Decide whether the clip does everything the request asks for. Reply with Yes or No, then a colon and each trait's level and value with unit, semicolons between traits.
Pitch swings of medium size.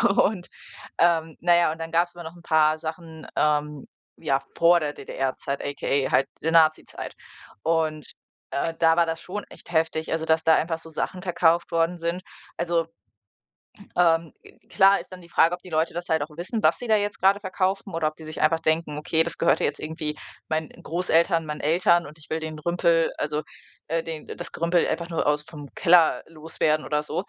No: narrow, 1.8 semitones